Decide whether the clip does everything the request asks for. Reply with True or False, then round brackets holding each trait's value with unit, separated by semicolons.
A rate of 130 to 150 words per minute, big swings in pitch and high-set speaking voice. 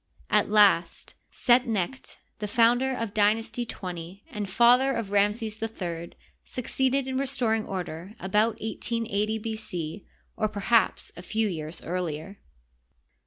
False (135 wpm; 3.5 semitones; 215 Hz)